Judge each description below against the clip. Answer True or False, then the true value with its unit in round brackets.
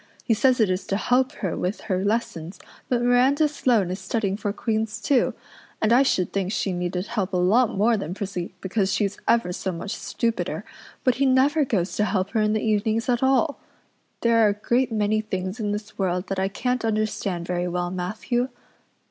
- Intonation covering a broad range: False (4.0 semitones)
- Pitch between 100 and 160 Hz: False (215 Hz)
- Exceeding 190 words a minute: True (200 wpm)